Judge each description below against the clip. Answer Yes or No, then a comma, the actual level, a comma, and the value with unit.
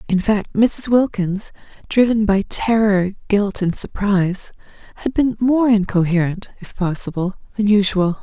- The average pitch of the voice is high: Yes, high, 205 Hz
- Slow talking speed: Yes, slow, 130 wpm